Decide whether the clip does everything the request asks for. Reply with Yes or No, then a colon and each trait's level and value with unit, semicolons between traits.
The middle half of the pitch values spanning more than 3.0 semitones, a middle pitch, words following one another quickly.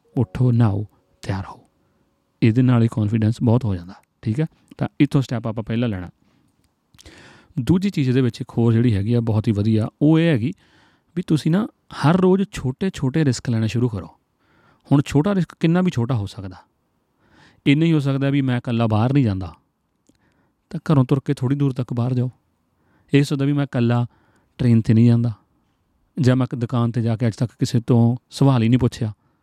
No: average, 3.7 semitones; low, 125 Hz; fast, 195 wpm